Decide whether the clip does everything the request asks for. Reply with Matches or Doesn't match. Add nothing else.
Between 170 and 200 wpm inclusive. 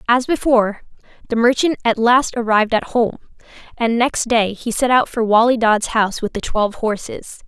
Matches